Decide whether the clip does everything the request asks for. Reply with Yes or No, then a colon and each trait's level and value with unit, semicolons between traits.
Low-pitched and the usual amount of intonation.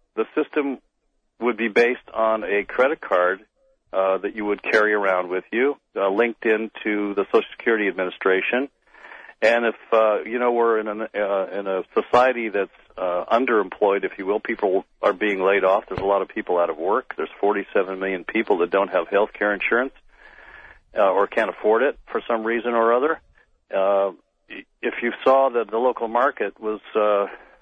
Yes: low, 110 Hz; average, 3.0 semitones